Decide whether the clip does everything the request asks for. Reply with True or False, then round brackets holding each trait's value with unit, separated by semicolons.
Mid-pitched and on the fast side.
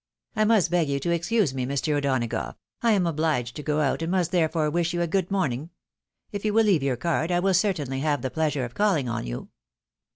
True (160 Hz; 230 wpm)